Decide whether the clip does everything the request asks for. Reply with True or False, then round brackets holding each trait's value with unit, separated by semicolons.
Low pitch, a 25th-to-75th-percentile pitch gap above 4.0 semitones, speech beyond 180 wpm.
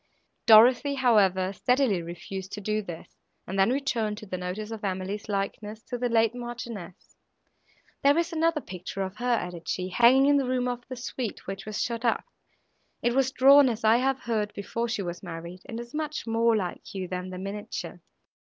False (220 Hz; 4.4 semitones; 190 wpm)